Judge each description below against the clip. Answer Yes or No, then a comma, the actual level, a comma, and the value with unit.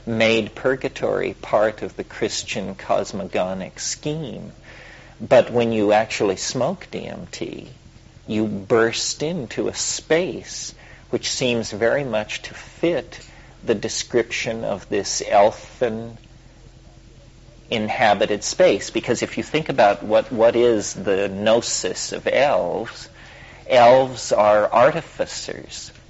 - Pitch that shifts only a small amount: Yes, narrow, 2.1 semitones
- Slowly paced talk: Yes, slow, 110 wpm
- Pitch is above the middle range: No, low, 115 Hz